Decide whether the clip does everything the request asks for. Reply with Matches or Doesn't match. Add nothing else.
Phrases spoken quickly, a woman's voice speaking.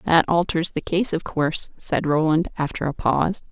Doesn't match